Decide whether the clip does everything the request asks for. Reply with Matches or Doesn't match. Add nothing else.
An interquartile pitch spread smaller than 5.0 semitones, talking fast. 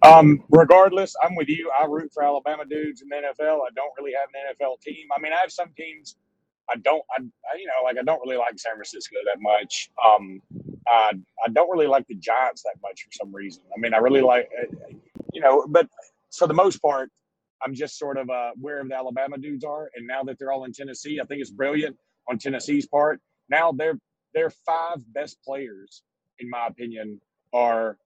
Matches